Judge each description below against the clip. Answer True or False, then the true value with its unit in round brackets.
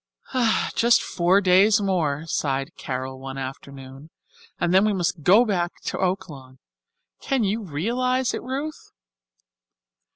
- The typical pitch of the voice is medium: True (180 Hz)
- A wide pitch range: True (7.5 semitones)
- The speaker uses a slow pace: True (125 wpm)